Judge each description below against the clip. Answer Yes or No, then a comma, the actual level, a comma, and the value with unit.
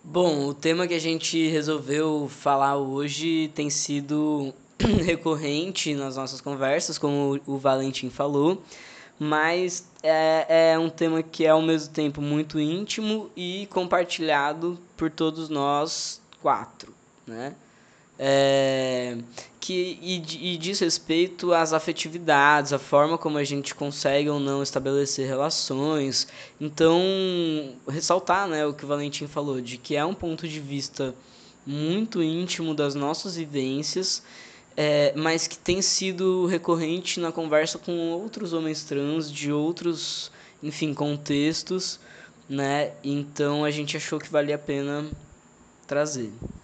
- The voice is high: No, medium, 155 Hz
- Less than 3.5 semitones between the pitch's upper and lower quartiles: Yes, average, 2.9 semitones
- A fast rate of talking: No, average, 130 wpm